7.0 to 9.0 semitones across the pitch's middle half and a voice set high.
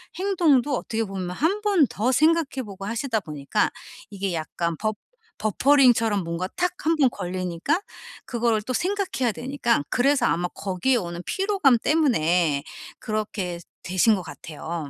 Yes: wide, 7.7 semitones; high, 220 Hz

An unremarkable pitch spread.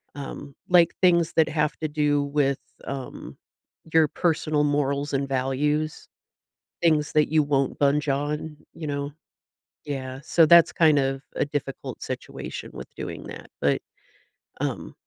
No: narrow, 1.8 semitones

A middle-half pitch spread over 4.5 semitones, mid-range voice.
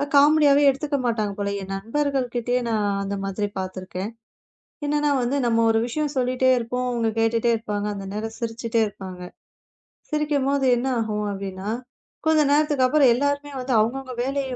No: average, 4.9 semitones; high, 240 Hz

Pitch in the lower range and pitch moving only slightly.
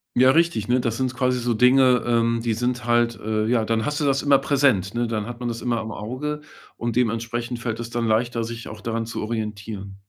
Yes: low, 120 Hz; narrow, 1.9 semitones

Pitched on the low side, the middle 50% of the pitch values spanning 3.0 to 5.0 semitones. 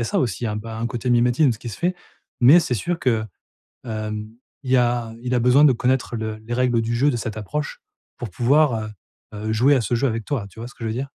No: low, 120 Hz; narrow, 2.5 semitones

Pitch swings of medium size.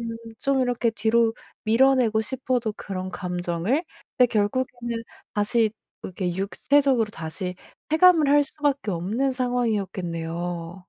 No: wide, 5.8 semitones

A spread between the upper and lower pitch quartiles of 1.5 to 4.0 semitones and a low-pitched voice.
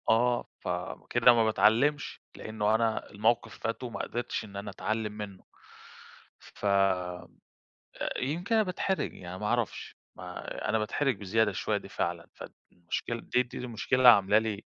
Yes: average, 3.2 semitones; low, 110 Hz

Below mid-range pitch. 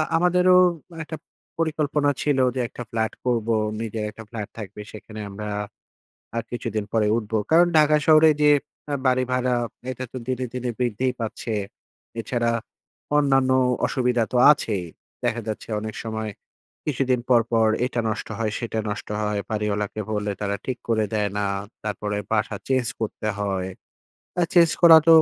Yes: low, 115 Hz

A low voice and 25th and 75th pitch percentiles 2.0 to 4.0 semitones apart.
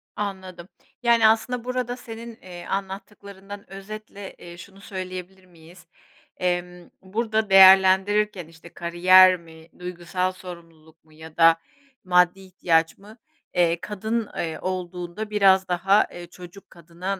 No: medium, 185 Hz; narrow, 2.6 semitones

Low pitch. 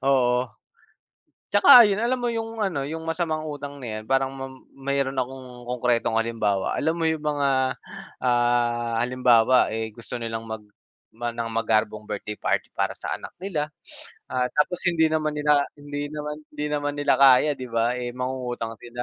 Yes: low, 130 Hz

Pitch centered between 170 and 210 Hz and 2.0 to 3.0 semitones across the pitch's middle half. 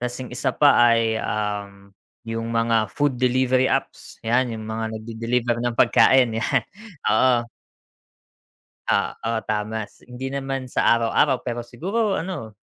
No: low, 120 Hz; narrow, 2.5 semitones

